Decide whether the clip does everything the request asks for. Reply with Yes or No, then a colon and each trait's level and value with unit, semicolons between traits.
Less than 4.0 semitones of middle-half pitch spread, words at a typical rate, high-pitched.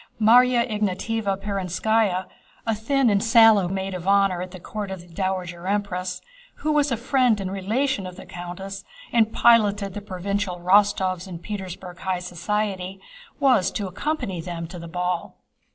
Yes: average, 3.1 semitones; average, 160 wpm; high, 195 Hz